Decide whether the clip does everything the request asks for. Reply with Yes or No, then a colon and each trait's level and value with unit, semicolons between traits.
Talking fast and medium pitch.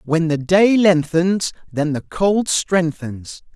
No: slow, 135 wpm; medium, 170 Hz